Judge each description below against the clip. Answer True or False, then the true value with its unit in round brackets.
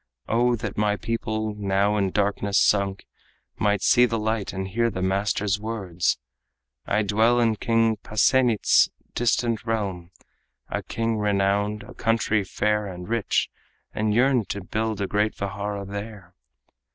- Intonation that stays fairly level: True (2.2 semitones)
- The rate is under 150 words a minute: True (140 wpm)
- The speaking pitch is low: True (105 Hz)